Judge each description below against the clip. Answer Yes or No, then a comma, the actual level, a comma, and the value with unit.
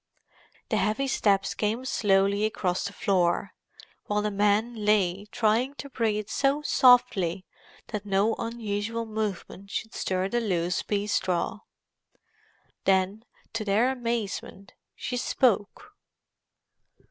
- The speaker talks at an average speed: No, slow, 115 wpm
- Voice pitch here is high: Yes, high, 210 Hz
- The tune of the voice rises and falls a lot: No, average, 2.8 semitones